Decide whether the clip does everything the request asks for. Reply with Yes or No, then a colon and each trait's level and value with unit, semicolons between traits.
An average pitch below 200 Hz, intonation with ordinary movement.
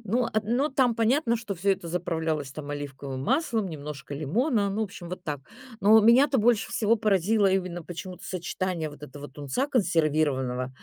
No: medium, 185 Hz; wide, 6.7 semitones